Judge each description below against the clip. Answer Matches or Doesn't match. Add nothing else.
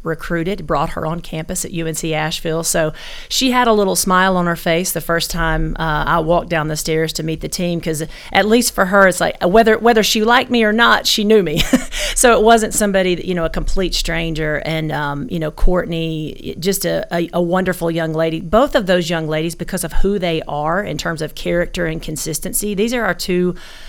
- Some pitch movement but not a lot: Matches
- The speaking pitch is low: Doesn't match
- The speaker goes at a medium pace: Doesn't match